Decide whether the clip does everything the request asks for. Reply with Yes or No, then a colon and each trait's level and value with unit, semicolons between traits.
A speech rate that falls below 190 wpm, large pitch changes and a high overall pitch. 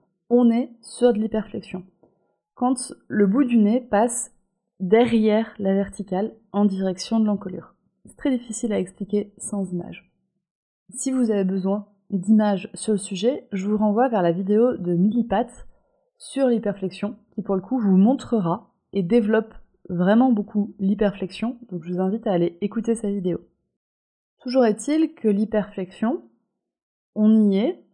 No: average, 150 wpm; average, 3.2 semitones; high, 210 Hz